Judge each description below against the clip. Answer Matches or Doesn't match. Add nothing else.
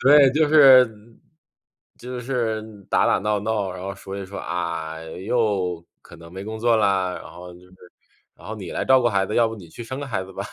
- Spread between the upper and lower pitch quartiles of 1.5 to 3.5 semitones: Doesn't match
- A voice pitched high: Doesn't match